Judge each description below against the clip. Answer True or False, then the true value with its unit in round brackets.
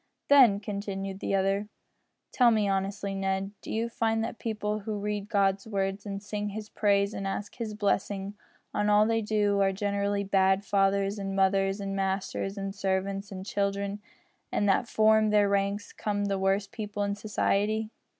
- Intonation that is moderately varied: False (1.3 semitones)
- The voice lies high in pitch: True (200 Hz)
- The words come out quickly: False (170 wpm)